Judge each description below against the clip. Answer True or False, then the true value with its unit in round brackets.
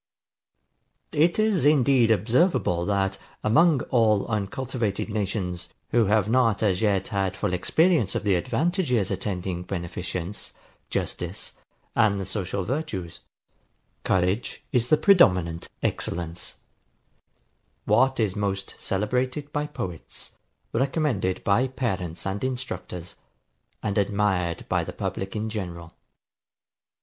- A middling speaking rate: False (110 wpm)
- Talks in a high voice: False (105 Hz)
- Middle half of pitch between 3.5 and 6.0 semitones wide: True (5.5 semitones)